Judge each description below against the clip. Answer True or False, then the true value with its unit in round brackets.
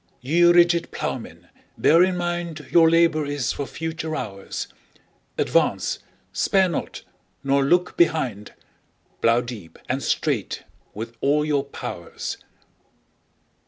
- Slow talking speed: True (110 wpm)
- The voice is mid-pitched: True (155 Hz)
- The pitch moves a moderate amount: True (4.8 semitones)